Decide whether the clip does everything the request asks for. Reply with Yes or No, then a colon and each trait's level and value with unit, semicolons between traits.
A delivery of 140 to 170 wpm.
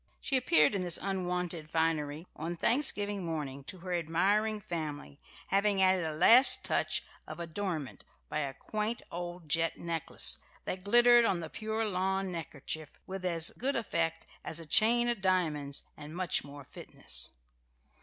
Yes: average, 155 wpm